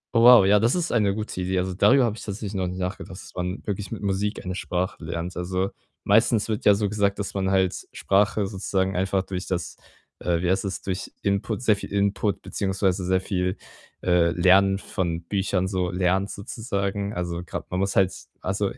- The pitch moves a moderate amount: No, narrow, 1.8 semitones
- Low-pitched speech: Yes, very low, 95 Hz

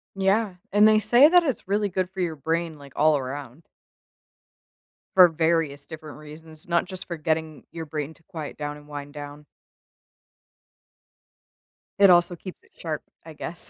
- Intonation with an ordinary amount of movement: Yes, average, 3.7 semitones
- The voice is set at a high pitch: No, medium, 160 Hz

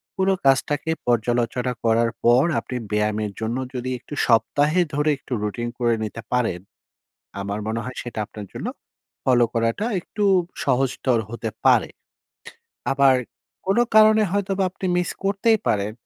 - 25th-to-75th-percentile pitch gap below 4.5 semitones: No, average, 5.0 semitones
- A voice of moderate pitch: No, low, 125 Hz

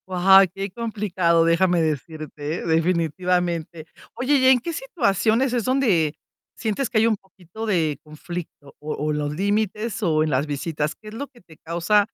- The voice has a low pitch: No, medium, 180 Hz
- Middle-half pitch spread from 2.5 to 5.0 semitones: No, wide, 5.4 semitones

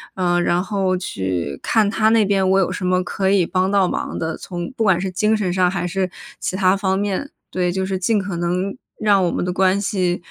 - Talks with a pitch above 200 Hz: No, high, 190 Hz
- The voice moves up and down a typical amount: No, narrow, 1.9 semitones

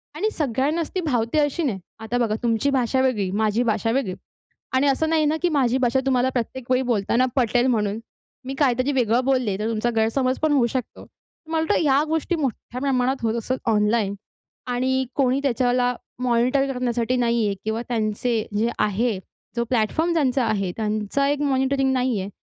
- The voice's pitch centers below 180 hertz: No, very high, 250 Hz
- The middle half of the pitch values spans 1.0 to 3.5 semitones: Yes, average, 3.1 semitones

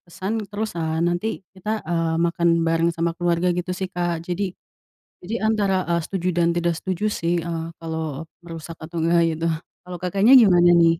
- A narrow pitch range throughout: Yes, narrow, 2.1 semitones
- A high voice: No, medium, 170 Hz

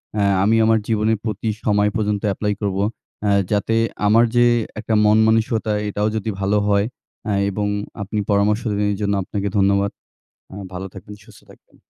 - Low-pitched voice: Yes, low, 105 Hz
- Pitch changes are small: Yes, narrow, 1.4 semitones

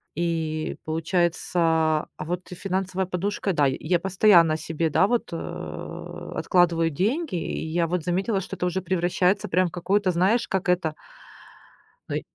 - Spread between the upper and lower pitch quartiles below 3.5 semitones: Yes, narrow, 2.5 semitones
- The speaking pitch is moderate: Yes, medium, 180 Hz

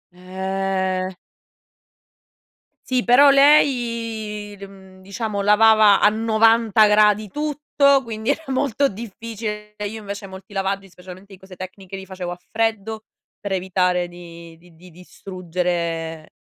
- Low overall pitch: No, high, 200 Hz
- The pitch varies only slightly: No, average, 3.1 semitones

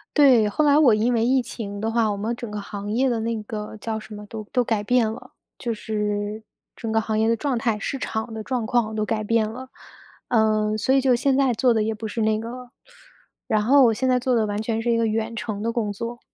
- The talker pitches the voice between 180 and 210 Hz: No, high, 225 Hz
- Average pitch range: No, narrow, 2.1 semitones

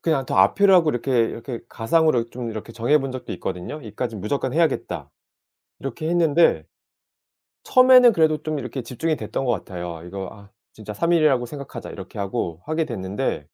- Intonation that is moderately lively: No, wide, 6.5 semitones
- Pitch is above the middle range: No, low, 125 Hz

